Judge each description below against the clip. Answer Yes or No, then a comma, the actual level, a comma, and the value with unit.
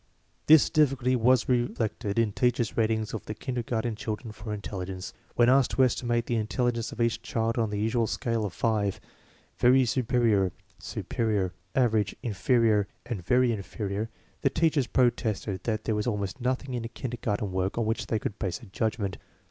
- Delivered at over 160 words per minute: Yes, average, 170 wpm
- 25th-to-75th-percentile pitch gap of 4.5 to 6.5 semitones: No, average, 2.7 semitones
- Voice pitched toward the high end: No, low, 115 Hz